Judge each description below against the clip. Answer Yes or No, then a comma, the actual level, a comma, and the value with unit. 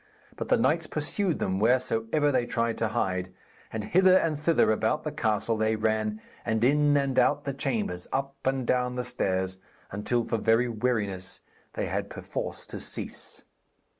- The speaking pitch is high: No, low, 115 Hz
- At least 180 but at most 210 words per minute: No, average, 165 wpm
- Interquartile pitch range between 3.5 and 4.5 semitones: Yes, average, 4.1 semitones